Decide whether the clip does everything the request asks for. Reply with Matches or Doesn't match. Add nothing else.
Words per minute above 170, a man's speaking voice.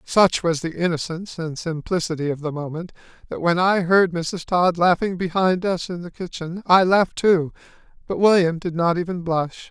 Matches